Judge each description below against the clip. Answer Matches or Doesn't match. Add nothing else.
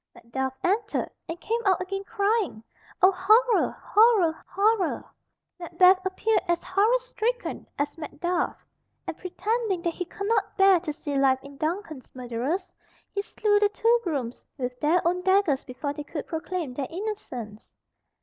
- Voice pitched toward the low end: Doesn't match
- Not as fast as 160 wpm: Matches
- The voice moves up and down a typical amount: Doesn't match